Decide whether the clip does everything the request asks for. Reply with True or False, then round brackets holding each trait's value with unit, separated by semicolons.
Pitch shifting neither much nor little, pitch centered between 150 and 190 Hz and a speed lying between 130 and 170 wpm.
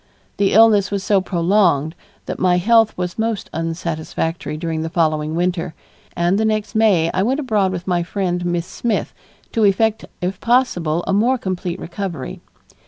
True (4.0 semitones; 185 Hz; 165 wpm)